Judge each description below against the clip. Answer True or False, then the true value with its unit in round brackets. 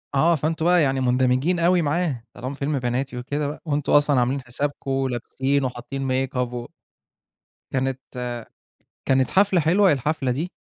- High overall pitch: False (135 Hz)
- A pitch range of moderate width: True (3.4 semitones)